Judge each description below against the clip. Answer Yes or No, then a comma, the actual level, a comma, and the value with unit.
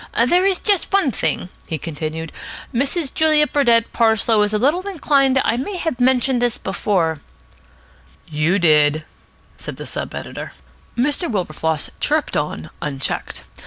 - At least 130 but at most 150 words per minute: Yes, average, 145 wpm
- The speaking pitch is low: No, high, 235 Hz